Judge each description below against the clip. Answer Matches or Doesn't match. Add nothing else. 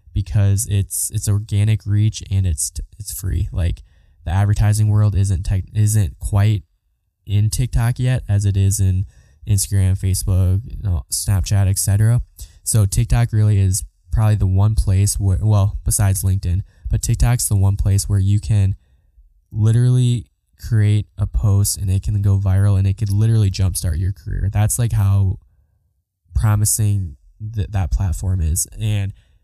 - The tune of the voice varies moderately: Doesn't match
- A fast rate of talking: Doesn't match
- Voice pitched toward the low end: Matches